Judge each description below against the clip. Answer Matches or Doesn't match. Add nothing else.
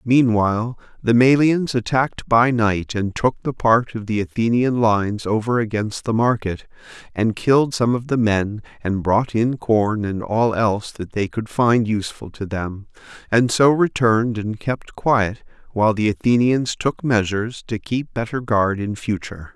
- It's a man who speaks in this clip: Matches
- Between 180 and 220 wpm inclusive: Doesn't match